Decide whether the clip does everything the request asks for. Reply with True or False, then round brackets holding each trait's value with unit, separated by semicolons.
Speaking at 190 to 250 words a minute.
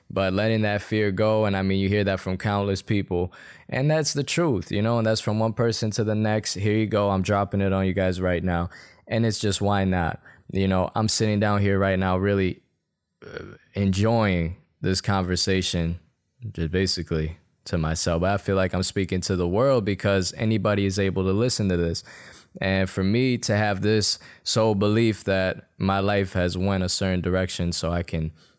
True (200 wpm)